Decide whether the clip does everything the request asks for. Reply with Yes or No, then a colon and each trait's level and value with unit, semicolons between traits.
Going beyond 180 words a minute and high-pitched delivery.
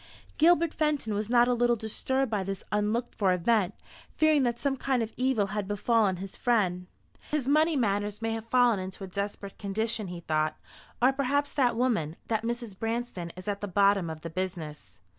Yes: average, 190 wpm; high, 220 Hz